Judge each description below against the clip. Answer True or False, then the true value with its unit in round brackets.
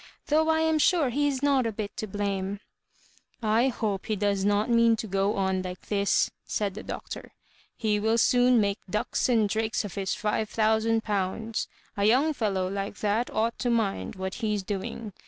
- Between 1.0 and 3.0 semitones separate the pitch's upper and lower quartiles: True (2.6 semitones)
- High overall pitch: True (215 Hz)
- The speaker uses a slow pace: False (190 wpm)